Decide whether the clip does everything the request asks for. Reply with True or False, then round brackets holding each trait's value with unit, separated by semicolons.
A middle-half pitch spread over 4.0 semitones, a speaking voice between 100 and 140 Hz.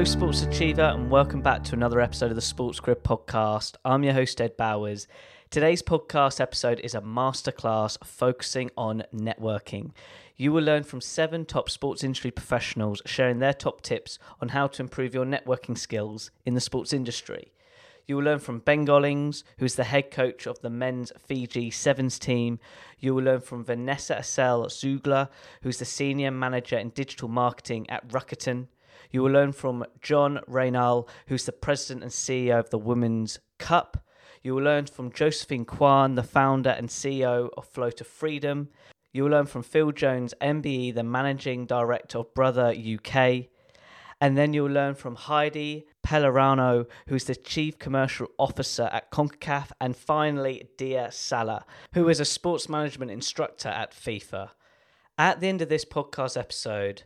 False (2.7 semitones; 130 Hz)